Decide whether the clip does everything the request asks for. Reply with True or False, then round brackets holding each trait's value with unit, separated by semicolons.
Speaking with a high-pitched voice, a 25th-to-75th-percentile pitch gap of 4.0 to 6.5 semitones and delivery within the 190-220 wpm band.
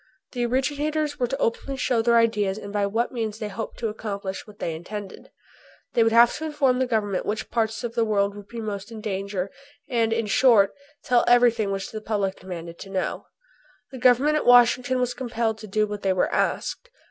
False (225 Hz; 3.3 semitones; 205 wpm)